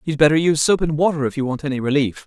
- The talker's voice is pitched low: No, medium, 145 Hz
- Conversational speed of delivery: No, fast, 290 wpm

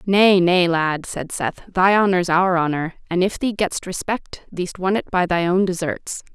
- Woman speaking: Yes, female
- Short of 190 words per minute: No, average, 200 wpm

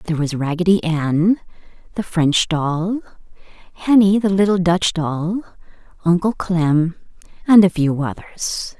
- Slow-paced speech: Yes, slow, 125 wpm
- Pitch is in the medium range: Yes, medium, 175 Hz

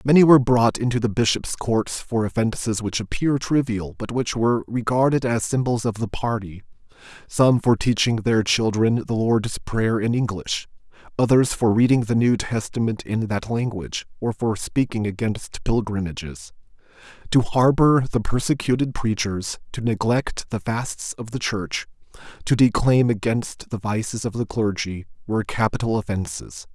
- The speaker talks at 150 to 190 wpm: Yes, average, 155 wpm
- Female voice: No, male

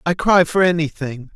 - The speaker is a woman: No, male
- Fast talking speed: No, average, 175 wpm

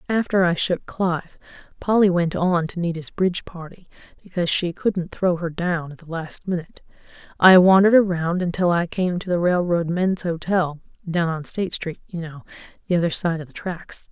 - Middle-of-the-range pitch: Yes, medium, 175 Hz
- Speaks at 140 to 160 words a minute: No, average, 180 wpm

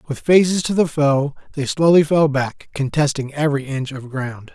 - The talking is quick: No, average, 185 wpm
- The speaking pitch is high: No, medium, 145 Hz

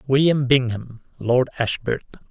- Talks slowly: Yes, slow, 105 wpm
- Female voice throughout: No, male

